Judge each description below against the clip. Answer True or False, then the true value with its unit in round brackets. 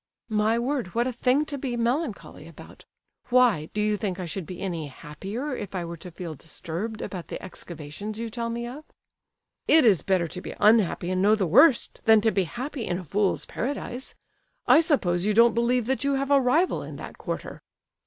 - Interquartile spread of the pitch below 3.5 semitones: False (5.3 semitones)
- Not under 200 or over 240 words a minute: True (205 wpm)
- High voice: True (220 Hz)